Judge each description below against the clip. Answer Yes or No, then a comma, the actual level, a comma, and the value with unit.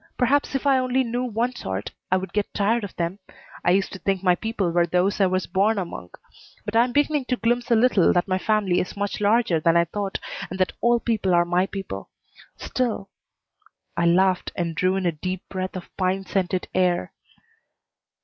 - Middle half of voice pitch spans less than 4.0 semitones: No, average, 4.3 semitones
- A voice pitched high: Yes, high, 195 Hz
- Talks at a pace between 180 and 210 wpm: Yes, fast, 205 wpm